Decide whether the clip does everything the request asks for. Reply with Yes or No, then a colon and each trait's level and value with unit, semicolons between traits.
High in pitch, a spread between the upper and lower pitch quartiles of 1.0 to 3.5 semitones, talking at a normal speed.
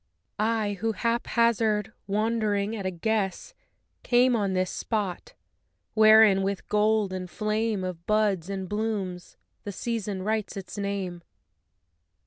No: high, 210 Hz; narrow, 2.4 semitones; slow, 120 wpm